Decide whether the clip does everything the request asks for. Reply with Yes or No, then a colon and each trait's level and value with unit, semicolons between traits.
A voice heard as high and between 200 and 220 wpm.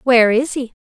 Yes: high, 245 Hz; fast, 215 wpm